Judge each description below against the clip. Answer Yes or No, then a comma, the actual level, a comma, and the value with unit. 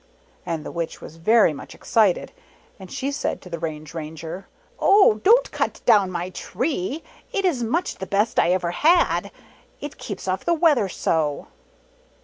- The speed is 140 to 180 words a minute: Yes, average, 170 wpm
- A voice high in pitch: Yes, high, 195 Hz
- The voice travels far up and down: Yes, wide, 8.9 semitones